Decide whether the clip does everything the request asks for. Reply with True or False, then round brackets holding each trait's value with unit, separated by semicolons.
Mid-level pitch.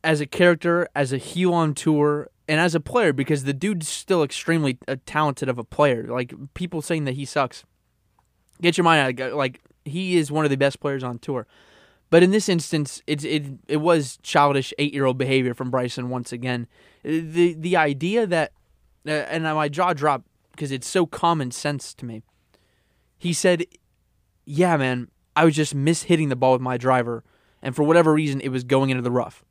True (145 Hz)